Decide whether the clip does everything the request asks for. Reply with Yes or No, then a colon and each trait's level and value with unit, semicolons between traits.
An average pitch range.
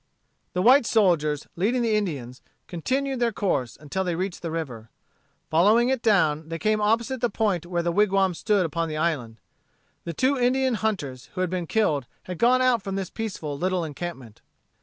No: wide, 5.9 semitones